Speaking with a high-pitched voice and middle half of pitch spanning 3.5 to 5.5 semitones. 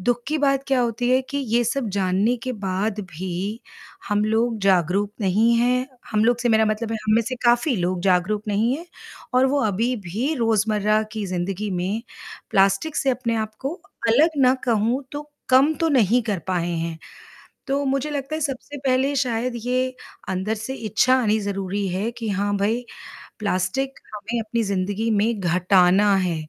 Yes: high, 220 Hz; average, 4.2 semitones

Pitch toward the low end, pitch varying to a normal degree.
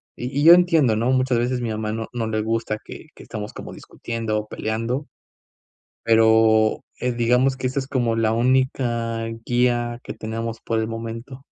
No: low, 115 Hz; narrow, 2.2 semitones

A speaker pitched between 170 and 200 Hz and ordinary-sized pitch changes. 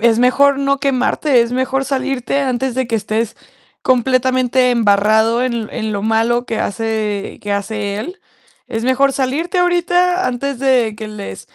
No: very high, 250 Hz; average, 3.5 semitones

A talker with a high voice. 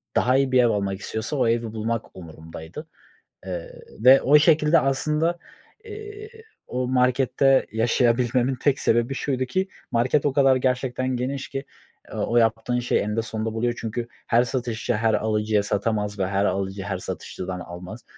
No: low, 120 Hz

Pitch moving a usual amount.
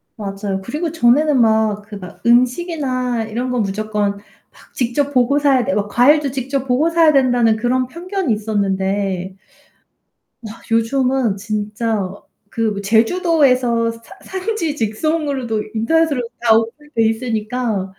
Yes: average, 4.5 semitones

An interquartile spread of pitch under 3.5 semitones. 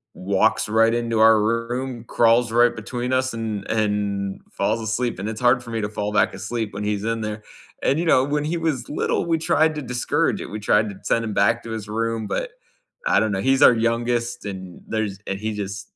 Yes: narrow, 2.6 semitones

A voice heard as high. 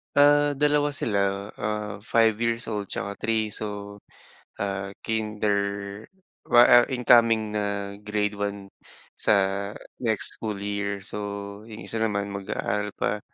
No: low, 105 Hz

